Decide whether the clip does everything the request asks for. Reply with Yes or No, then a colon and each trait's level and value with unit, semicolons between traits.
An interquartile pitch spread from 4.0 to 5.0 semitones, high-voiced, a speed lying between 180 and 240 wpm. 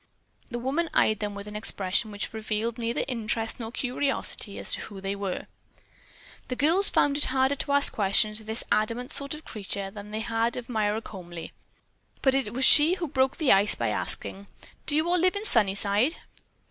Yes: average, 4.7 semitones; high, 225 Hz; average, 200 wpm